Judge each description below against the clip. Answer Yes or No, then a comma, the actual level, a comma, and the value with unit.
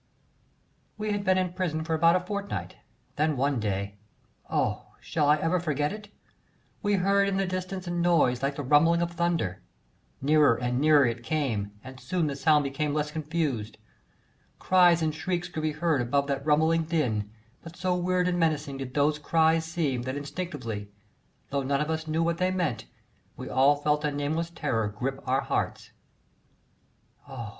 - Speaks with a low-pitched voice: No, medium, 155 Hz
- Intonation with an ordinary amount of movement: Yes, average, 3.9 semitones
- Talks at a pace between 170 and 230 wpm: Yes, average, 175 wpm